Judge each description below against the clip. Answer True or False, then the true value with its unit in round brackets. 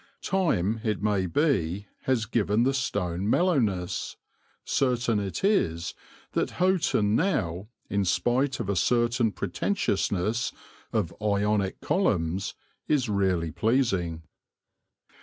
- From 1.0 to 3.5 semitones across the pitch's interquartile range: False (5.2 semitones)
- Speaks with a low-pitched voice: True (105 Hz)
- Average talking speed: False (105 wpm)